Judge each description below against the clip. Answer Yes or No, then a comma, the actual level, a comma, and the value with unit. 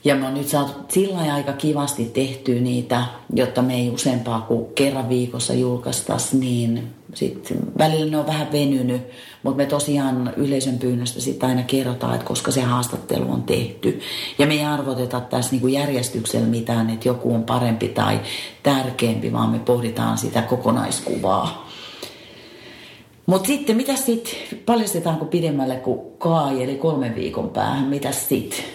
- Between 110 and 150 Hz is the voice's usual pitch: Yes, low, 130 Hz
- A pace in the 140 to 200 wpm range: Yes, average, 150 wpm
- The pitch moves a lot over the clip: No, average, 2.8 semitones